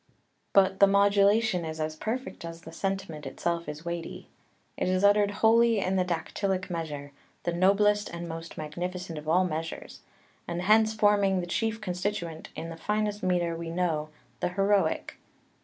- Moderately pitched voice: Yes, medium, 180 Hz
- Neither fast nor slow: Yes, average, 160 wpm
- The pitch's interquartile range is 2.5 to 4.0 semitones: Yes, average, 3.5 semitones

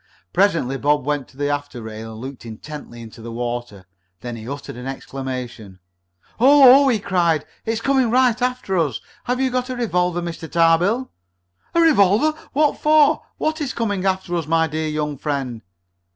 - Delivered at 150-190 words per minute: Yes, average, 170 wpm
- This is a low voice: No, medium, 165 Hz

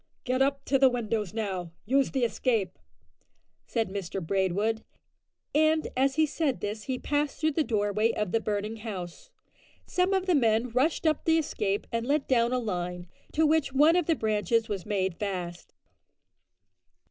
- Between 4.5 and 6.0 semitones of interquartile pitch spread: Yes, wide, 5.5 semitones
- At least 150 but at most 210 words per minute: Yes, average, 170 wpm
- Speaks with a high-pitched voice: Yes, high, 230 Hz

